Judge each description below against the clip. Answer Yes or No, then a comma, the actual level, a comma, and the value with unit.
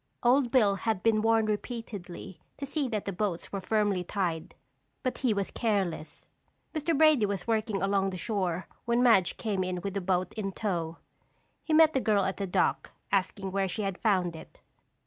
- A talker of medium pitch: No, high, 200 Hz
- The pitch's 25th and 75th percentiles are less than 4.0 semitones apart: Yes, average, 3.4 semitones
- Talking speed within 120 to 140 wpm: No, average, 185 wpm